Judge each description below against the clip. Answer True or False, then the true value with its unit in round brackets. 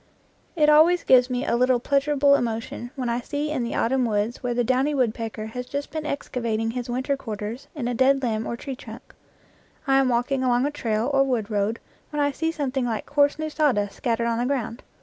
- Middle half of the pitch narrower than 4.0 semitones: True (3.3 semitones)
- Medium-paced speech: False (220 wpm)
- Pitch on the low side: False (250 Hz)